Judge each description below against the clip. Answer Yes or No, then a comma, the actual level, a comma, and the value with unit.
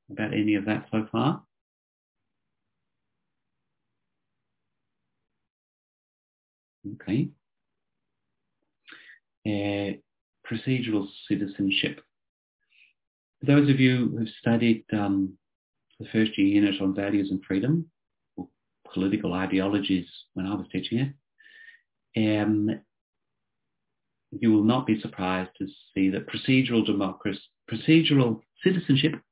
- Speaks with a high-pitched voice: No, low, 105 Hz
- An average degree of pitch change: Yes, average, 4.6 semitones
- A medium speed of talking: No, slow, 95 wpm